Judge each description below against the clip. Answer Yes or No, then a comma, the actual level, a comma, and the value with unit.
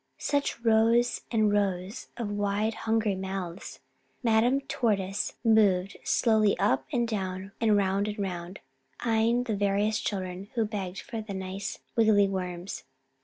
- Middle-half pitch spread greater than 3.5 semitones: No, average, 2.7 semitones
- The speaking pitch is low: No, high, 205 Hz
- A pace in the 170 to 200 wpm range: No, slow, 135 wpm